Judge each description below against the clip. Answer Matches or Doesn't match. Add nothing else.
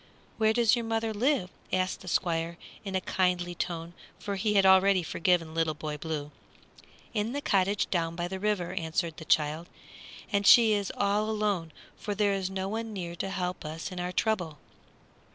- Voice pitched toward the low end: Doesn't match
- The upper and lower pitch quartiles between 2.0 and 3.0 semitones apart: Doesn't match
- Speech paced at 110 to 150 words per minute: Doesn't match